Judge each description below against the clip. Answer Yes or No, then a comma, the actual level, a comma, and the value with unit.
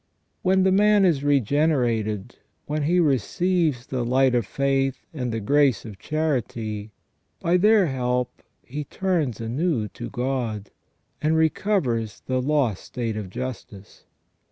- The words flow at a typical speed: No, slow, 130 wpm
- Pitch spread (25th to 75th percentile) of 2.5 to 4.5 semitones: No, average, 5.2 semitones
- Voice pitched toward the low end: Yes, low, 130 Hz